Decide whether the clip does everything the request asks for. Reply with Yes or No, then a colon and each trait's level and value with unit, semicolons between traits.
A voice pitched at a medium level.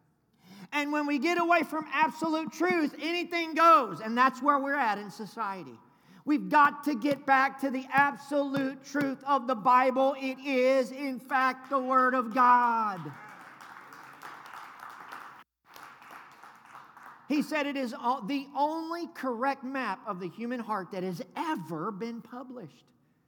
No: very high, 270 Hz